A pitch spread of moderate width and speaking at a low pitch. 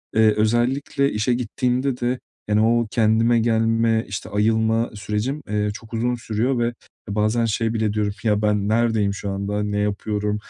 No: narrow, 2.0 semitones; low, 110 Hz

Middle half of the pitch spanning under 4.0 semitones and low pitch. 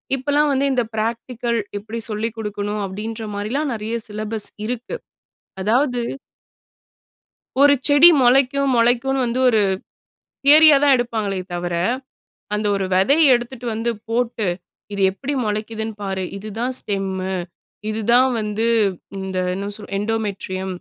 No: average, 3.3 semitones; high, 225 Hz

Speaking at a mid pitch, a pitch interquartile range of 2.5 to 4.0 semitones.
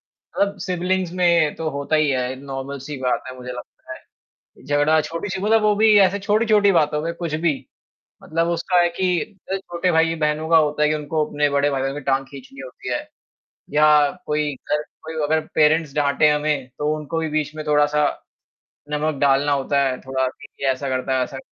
Yes: medium, 150 Hz; average, 2.9 semitones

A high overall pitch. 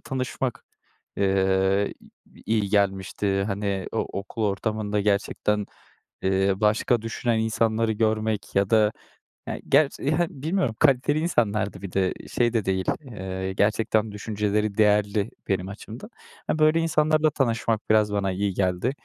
No: low, 105 Hz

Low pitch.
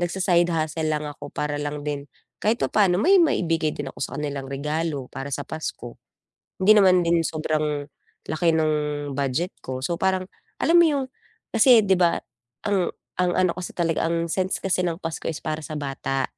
No: medium, 165 Hz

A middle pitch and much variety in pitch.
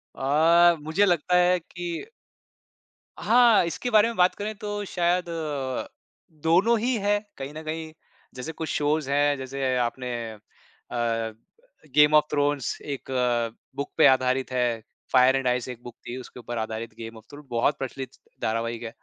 Yes: medium, 145 Hz; wide, 5.7 semitones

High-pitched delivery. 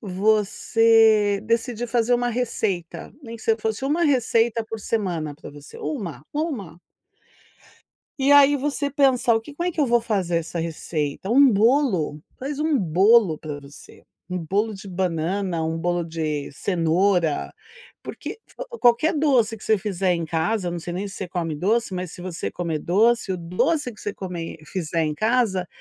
Yes: high, 200 Hz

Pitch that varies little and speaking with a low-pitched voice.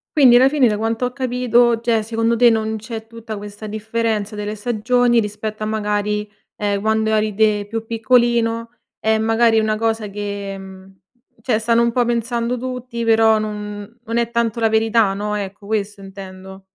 No: narrow, 1.9 semitones; high, 220 Hz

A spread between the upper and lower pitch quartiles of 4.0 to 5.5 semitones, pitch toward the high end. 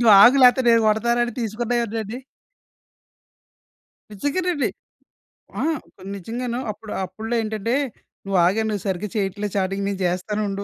No: average, 3.2 semitones; high, 215 Hz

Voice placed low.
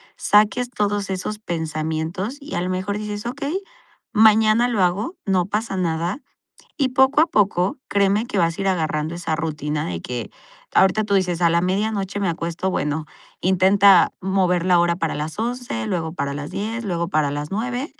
No: high, 190 Hz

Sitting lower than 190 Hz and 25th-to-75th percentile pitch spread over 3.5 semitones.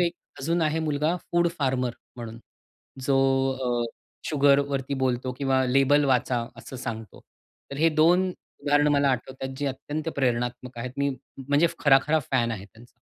No: low, 135 Hz; average, 2.7 semitones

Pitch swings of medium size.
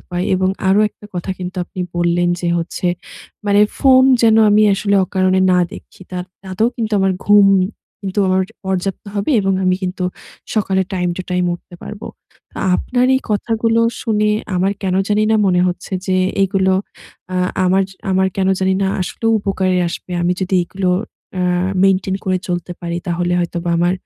No: narrow, 2.0 semitones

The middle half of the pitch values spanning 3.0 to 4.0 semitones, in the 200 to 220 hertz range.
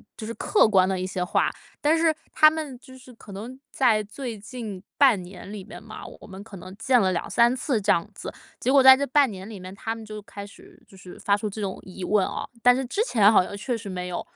No: average, 4.7 semitones; high, 215 Hz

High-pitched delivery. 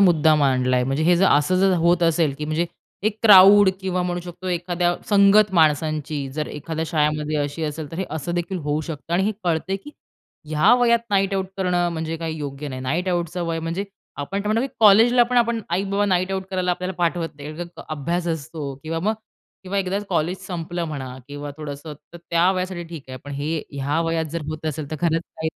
No: medium, 170 Hz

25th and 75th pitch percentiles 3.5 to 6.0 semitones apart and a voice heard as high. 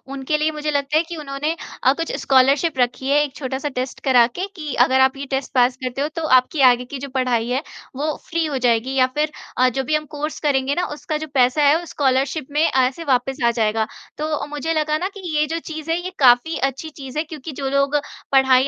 No: average, 2.9 semitones; very high, 280 Hz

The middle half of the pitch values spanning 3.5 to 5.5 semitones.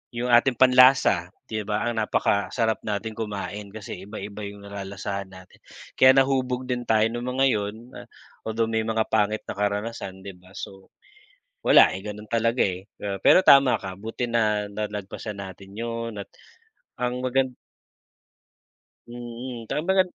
No: average, 3.1 semitones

